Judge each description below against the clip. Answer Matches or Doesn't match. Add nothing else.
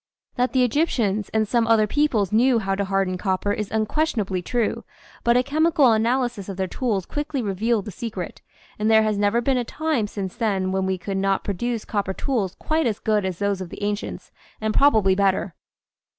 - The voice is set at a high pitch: Matches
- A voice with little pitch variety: Doesn't match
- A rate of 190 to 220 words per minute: Matches